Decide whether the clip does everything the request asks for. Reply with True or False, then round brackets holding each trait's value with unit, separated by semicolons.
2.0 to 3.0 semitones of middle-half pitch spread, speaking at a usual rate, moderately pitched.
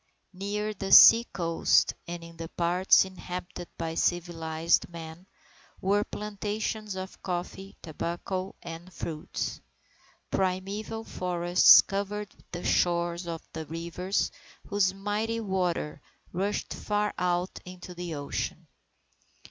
False (2.7 semitones; 110 wpm; 180 Hz)